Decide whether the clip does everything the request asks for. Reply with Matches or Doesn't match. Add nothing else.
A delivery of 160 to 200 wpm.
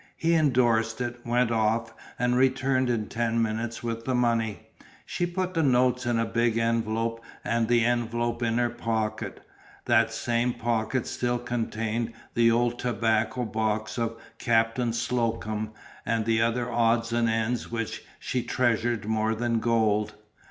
Doesn't match